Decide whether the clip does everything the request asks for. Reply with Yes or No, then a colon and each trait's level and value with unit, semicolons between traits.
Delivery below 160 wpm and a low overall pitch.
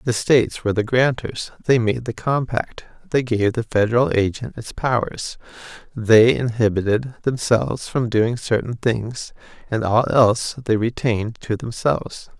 Yes: average, 145 wpm; low, 115 Hz